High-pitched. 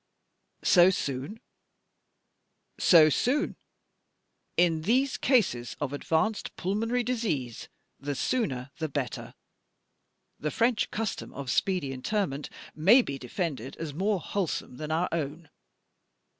No: medium, 165 Hz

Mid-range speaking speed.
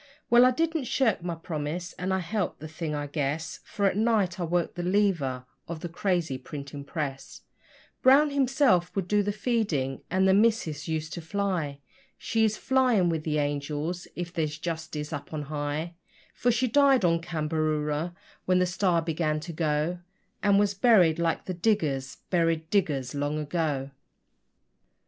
Yes: average, 165 wpm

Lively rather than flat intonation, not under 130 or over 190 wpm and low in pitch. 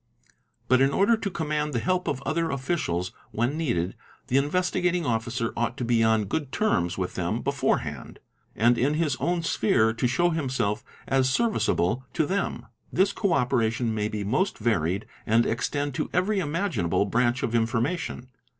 Yes: wide, 6.6 semitones; average, 170 wpm; low, 130 Hz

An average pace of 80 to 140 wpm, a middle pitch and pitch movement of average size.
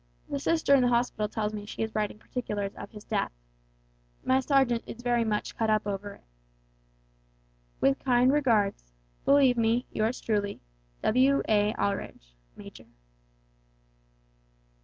No: slow, 135 wpm; high, 220 Hz; average, 3.3 semitones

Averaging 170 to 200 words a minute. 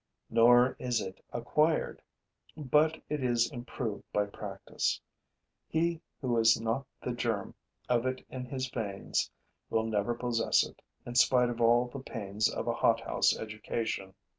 No: average, 145 wpm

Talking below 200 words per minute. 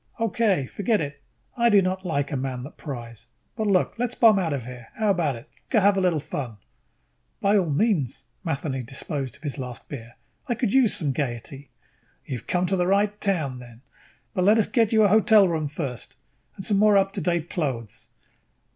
No: fast, 205 wpm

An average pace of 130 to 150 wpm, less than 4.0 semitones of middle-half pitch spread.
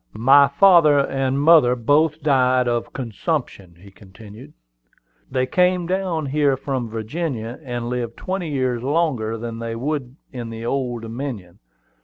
No: average, 140 wpm; average, 4.4 semitones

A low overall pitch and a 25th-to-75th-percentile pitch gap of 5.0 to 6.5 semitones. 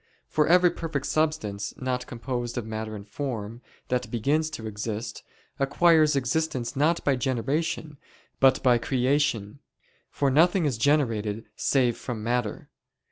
No: low, 130 Hz; average, 4.6 semitones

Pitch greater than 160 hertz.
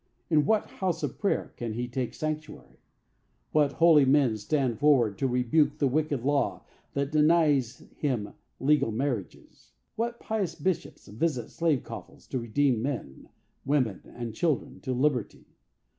No: medium, 140 Hz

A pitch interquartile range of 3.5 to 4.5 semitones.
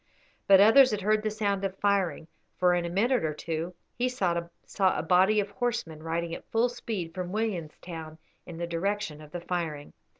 Yes: average, 4.0 semitones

